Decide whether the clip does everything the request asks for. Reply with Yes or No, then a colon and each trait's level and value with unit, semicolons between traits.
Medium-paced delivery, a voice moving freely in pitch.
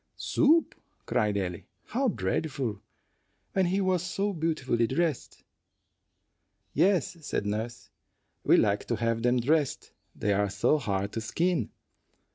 No: slow, 125 wpm; wide, 8.5 semitones